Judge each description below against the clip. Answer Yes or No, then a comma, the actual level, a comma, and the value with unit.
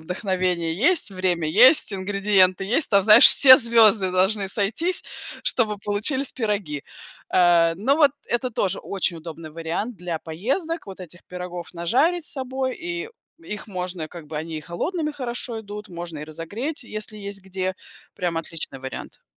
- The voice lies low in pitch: No, high, 195 Hz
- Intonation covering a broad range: Yes, wide, 5.7 semitones